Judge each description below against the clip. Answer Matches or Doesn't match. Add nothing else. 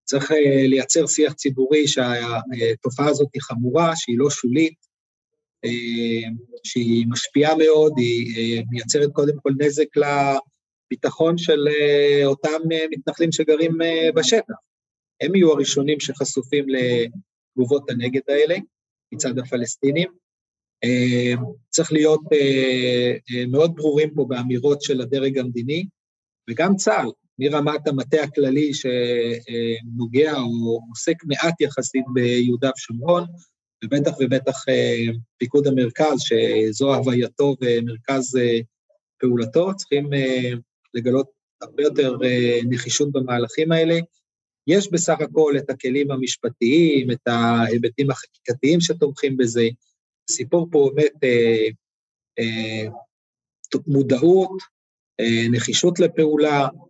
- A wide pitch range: Doesn't match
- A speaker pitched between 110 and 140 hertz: Matches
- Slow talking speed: Matches